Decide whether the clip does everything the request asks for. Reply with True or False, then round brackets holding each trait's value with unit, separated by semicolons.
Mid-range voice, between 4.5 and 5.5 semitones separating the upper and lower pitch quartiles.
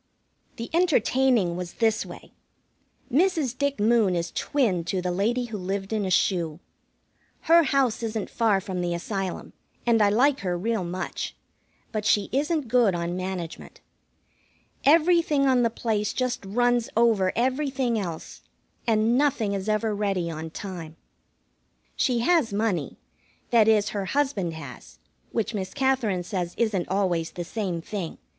False (215 Hz; 5.0 semitones)